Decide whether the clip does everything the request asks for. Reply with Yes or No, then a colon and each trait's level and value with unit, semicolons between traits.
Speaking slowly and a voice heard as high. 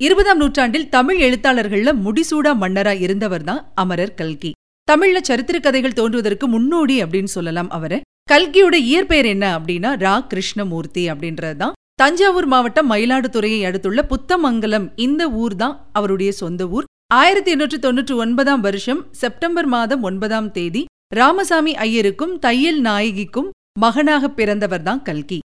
No: average, 125 wpm; high, 245 Hz